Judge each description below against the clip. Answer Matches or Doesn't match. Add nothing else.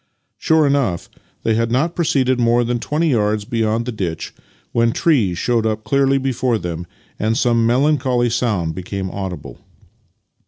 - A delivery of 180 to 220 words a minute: Doesn't match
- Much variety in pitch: Doesn't match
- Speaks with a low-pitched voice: Matches